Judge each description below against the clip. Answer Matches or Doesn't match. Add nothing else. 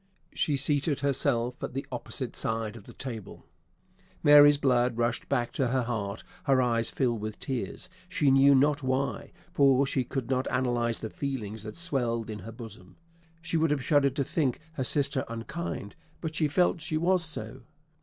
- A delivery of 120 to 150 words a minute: Doesn't match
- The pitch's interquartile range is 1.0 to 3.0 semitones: Doesn't match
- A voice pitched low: Matches